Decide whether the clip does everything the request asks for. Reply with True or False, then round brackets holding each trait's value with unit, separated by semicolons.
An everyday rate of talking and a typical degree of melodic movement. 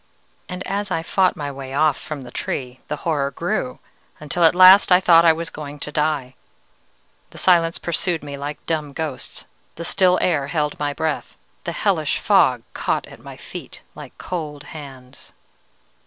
True (170 wpm; 3.2 semitones)